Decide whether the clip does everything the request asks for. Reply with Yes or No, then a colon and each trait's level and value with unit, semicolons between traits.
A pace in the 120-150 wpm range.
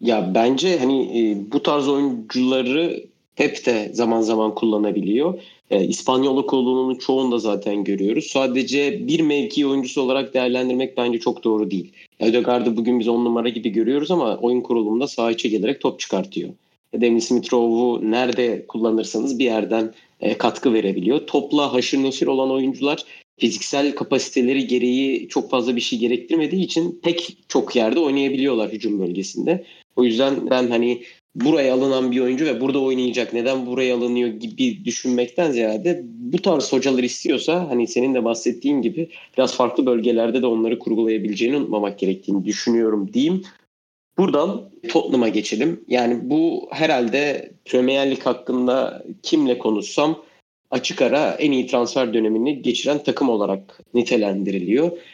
Yes: fast, 140 wpm